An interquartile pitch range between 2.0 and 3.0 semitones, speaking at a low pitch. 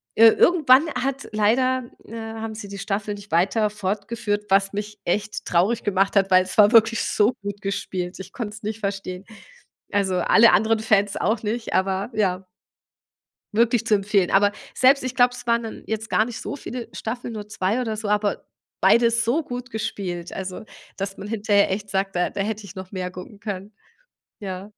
No: average, 2.7 semitones; high, 210 Hz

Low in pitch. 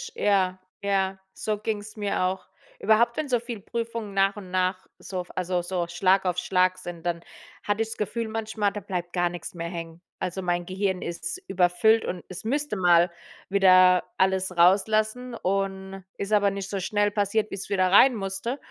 No: high, 195 Hz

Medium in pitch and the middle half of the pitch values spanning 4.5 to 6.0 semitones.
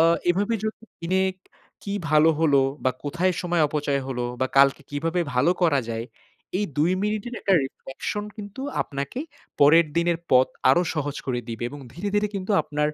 Yes: medium, 160 Hz; average, 5.1 semitones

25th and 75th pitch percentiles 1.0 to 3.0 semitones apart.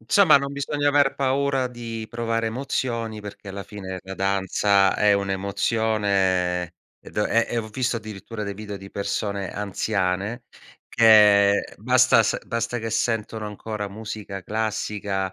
Yes: narrow, 2.6 semitones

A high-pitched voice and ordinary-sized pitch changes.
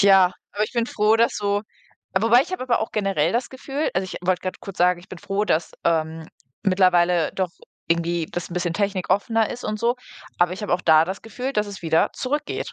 Yes: high, 195 Hz; average, 4.2 semitones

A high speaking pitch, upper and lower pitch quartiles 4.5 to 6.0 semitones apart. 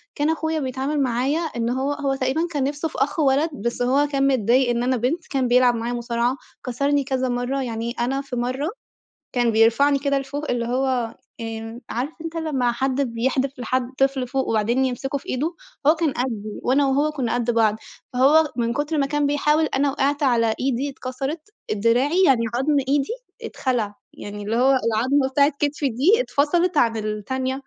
No: very high, 265 Hz; average, 3.1 semitones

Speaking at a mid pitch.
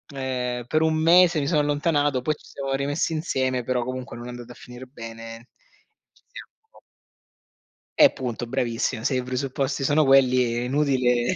No: low, 130 Hz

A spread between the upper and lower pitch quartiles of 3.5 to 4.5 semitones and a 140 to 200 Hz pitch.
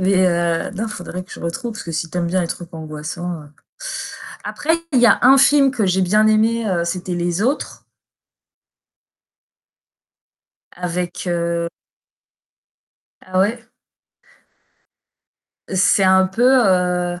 Yes: average, 3.8 semitones; medium, 185 Hz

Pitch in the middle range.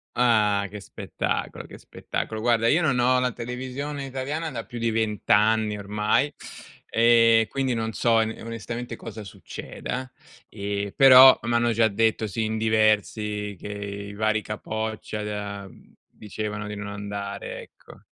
No: low, 110 Hz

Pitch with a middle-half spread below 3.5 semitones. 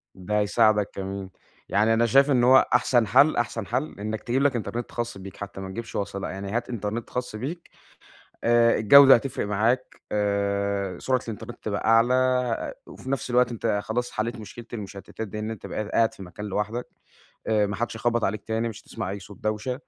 Yes: average, 3.0 semitones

